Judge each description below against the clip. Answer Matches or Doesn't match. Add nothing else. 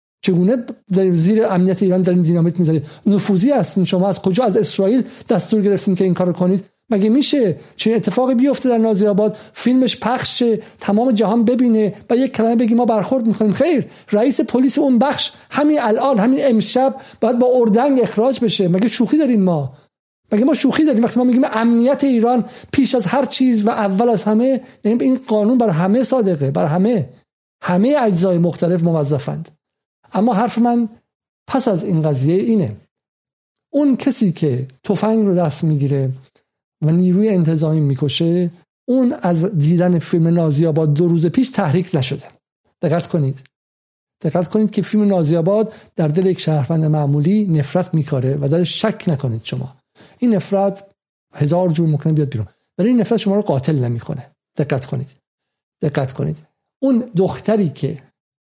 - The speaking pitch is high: Matches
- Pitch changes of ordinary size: Doesn't match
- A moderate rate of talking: Doesn't match